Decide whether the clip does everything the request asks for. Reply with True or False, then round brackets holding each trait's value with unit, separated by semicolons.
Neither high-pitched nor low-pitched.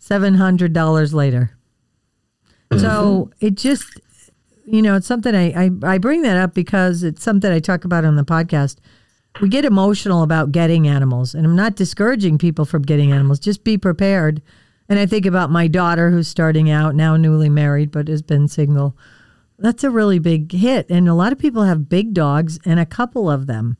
True (170 Hz)